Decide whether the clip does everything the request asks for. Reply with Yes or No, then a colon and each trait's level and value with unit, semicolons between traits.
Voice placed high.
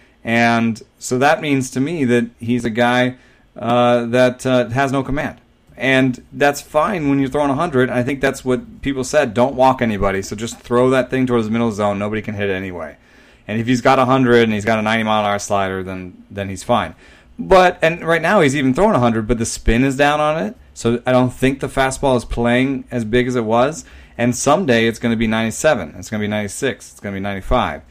No: low, 125 Hz